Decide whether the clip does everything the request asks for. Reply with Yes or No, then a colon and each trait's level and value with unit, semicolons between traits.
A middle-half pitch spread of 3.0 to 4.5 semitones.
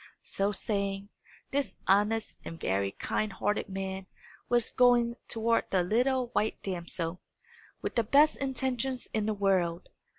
Yes: average, 4.1 semitones